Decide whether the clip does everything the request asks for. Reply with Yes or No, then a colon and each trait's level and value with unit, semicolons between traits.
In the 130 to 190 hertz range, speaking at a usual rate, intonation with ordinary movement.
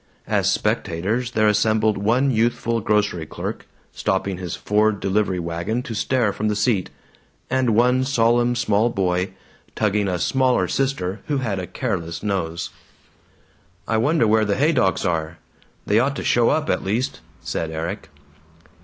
No: low, 105 Hz; average, 150 wpm; average, 4.2 semitones